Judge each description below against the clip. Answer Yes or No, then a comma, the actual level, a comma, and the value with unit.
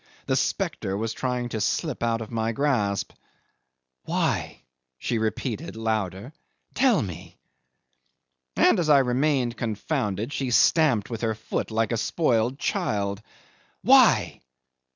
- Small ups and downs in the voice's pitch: No, average, 3.9 semitones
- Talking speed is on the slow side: Yes, slow, 125 wpm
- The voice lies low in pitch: Yes, low, 115 Hz